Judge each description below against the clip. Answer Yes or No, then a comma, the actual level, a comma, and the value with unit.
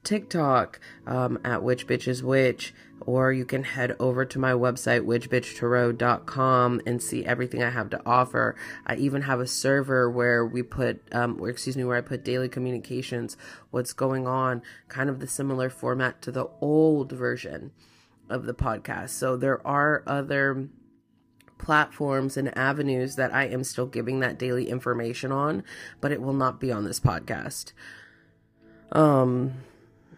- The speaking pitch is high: No, low, 125 Hz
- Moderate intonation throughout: No, narrow, 1.6 semitones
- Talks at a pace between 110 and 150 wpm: No, average, 160 wpm